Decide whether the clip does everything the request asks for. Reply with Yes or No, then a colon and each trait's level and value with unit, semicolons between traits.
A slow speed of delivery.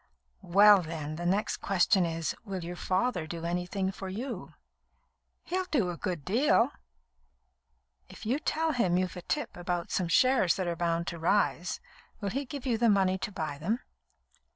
No: average, 175 wpm